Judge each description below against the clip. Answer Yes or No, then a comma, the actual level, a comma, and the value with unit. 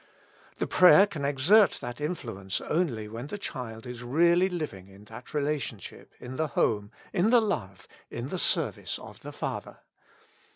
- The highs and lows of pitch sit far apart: Yes, wide, 7.5 semitones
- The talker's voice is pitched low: Yes, low, 130 Hz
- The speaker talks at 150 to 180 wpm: Yes, average, 160 wpm